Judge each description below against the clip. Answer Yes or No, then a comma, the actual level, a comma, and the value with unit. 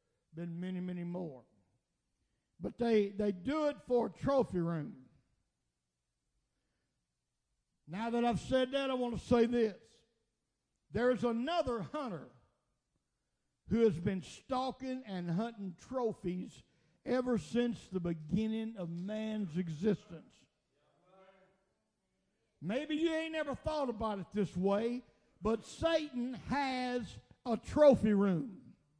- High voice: Yes, high, 220 Hz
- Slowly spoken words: Yes, slow, 115 wpm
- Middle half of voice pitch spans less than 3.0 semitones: No, wide, 5.5 semitones